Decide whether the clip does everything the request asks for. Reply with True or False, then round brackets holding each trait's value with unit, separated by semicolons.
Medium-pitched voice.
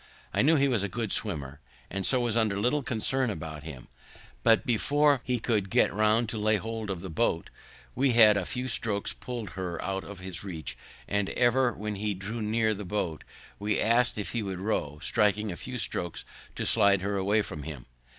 False (105 Hz)